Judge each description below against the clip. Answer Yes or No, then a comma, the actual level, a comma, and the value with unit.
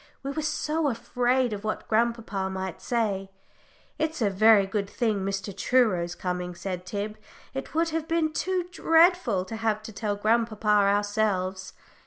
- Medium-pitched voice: No, high, 215 Hz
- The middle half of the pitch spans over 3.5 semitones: Yes, average, 4.7 semitones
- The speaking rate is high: No, average, 160 wpm